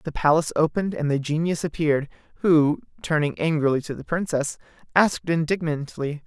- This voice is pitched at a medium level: Yes, medium, 155 Hz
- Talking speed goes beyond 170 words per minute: No, average, 145 wpm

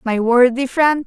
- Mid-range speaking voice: No, very high, 255 Hz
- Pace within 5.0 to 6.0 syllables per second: No, 4.1 syllables/s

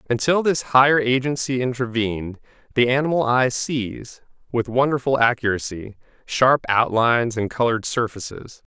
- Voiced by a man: Yes, male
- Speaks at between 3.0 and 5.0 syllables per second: Yes, 4.9 syllables/s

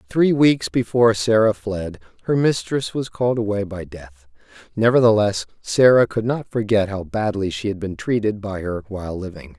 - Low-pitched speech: Yes, low, 105 Hz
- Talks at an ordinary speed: Yes, average, 170 wpm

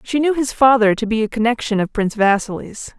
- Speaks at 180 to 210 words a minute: No, fast, 220 wpm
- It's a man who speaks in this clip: No, female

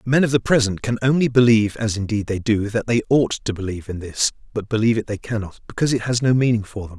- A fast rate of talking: Yes, fast, 260 wpm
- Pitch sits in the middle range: No, low, 110 Hz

